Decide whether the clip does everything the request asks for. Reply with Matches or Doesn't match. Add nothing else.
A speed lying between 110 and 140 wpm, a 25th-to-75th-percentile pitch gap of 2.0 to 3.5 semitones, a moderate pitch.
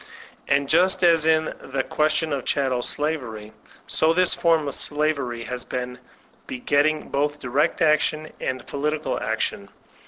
Matches